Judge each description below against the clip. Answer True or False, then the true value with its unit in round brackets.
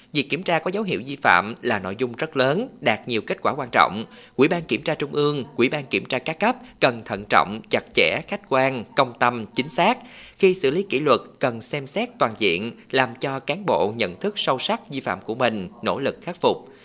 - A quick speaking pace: False (240 wpm)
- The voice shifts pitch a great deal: True (7.6 semitones)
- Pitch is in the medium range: True (145 Hz)